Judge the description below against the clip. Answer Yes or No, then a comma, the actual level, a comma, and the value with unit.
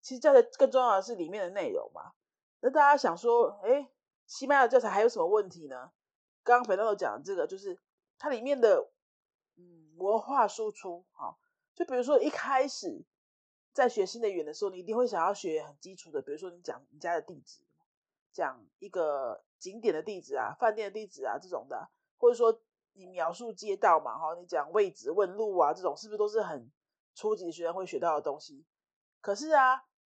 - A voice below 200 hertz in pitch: No, high, 245 Hz